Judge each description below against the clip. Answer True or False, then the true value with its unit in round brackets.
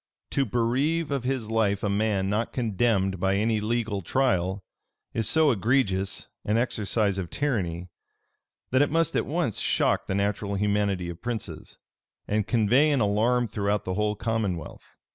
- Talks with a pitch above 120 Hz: False (105 Hz)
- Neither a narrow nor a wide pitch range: True (3.6 semitones)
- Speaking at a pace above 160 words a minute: False (155 wpm)